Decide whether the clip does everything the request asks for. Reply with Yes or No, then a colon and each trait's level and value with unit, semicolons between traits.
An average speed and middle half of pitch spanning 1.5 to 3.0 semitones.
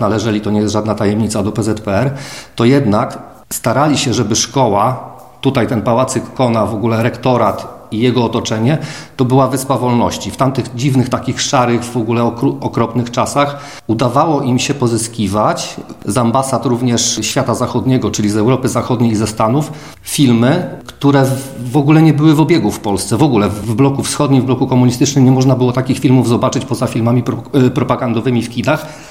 No: fast, 175 wpm; average, 2.7 semitones